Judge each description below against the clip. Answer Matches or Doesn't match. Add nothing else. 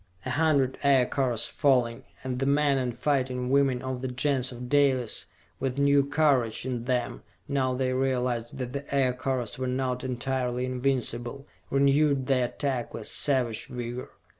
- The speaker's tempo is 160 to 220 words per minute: Doesn't match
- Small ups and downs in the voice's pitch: Matches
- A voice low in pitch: Matches